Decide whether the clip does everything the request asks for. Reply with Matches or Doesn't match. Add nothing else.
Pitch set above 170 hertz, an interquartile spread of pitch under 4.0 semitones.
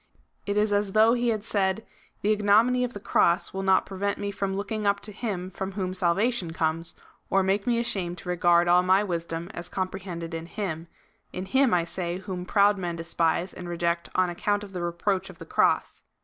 Matches